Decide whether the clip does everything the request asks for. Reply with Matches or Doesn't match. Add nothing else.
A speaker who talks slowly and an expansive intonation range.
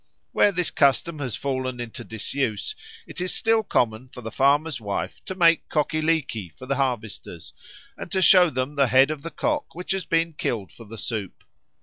Doesn't match